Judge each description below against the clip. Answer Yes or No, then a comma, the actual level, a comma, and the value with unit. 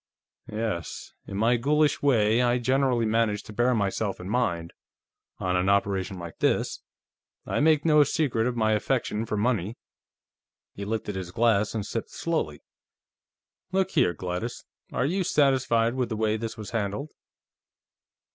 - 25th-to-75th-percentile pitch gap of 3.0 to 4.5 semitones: Yes, average, 3.9 semitones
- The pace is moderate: Yes, average, 150 wpm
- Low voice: Yes, low, 115 Hz